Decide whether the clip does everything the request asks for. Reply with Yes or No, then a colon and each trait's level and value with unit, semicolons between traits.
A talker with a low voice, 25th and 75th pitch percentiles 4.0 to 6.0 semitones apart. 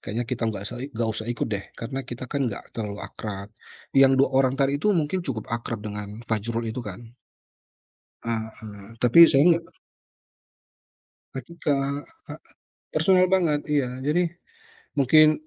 Yes: low, 125 Hz; average, 4.5 semitones